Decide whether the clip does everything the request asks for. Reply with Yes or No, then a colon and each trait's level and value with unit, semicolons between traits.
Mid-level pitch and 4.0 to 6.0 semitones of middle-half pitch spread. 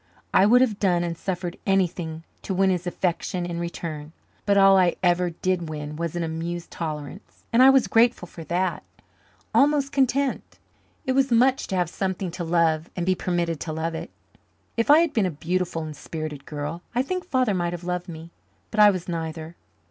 No: medium, 175 Hz; average, 3.4 semitones